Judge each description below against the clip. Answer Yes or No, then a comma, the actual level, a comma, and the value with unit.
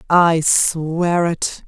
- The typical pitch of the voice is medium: Yes, medium, 165 Hz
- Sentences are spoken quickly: No, slow, 105 wpm